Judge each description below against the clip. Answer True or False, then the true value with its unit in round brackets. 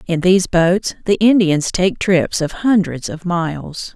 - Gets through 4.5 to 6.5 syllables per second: False (4.1 syllables/s)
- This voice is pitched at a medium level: True (175 Hz)